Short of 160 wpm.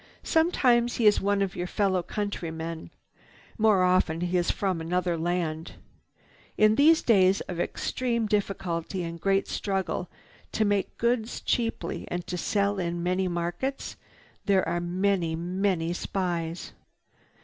Yes: slow, 135 wpm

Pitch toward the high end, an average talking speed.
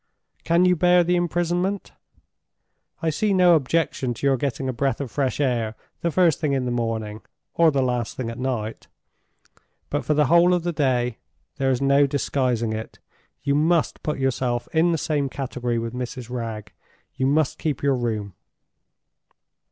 No: low, 135 Hz; average, 170 wpm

